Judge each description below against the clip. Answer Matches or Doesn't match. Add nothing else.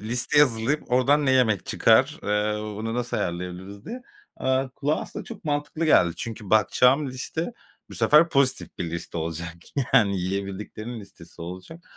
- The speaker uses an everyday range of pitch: Doesn't match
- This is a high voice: Doesn't match